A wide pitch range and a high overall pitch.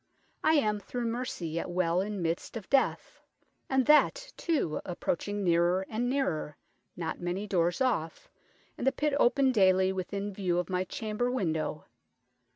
Yes: wide, 5.8 semitones; high, 195 Hz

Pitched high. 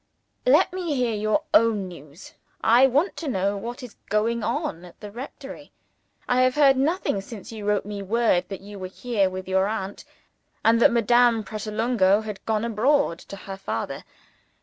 Yes: high, 215 Hz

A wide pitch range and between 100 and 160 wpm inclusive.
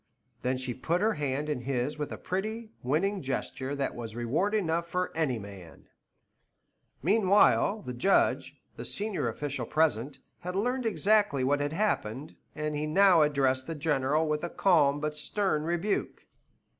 Yes: wide, 6.1 semitones; average, 155 wpm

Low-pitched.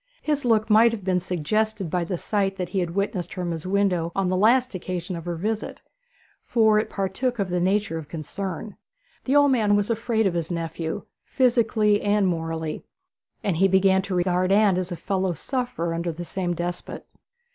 No: high, 190 Hz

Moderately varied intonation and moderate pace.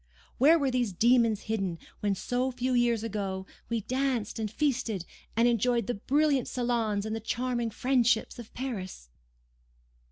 Yes: average, 3.0 semitones; average, 150 wpm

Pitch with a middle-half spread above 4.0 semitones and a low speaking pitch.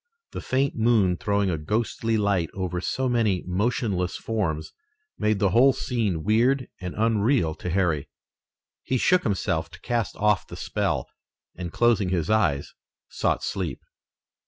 Yes: average, 4.5 semitones; low, 105 Hz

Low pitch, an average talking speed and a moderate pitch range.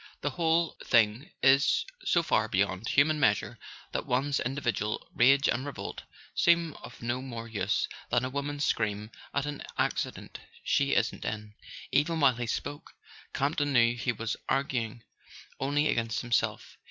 Yes: low, 130 Hz; average, 155 wpm; average, 4.0 semitones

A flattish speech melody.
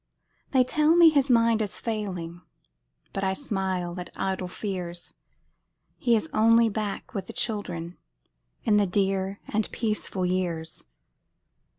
No: average, 3.8 semitones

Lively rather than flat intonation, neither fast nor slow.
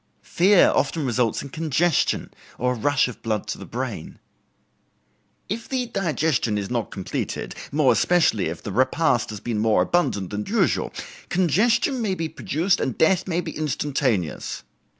Yes: wide, 7.7 semitones; average, 150 wpm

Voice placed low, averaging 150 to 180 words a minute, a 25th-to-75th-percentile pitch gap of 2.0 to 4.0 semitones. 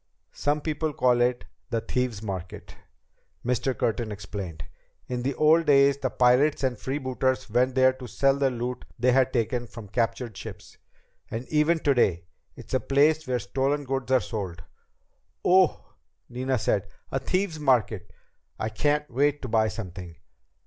Yes: low, 125 Hz; average, 155 wpm; average, 3.7 semitones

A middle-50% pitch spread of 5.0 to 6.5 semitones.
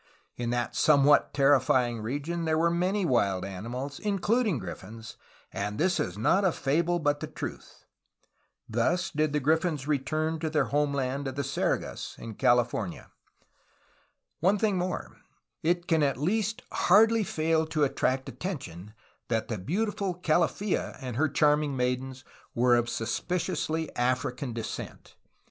Yes: wide, 5.5 semitones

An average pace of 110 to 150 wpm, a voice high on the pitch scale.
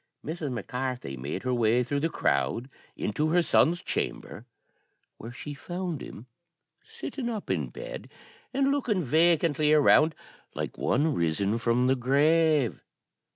No: average, 145 wpm; medium, 145 Hz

